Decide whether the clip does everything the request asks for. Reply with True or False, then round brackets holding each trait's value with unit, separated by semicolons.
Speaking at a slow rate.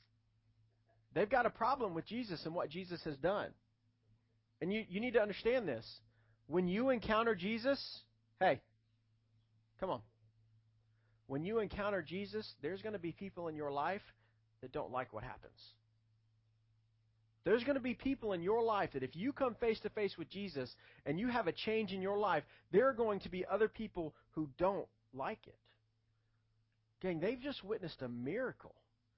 False (175 wpm)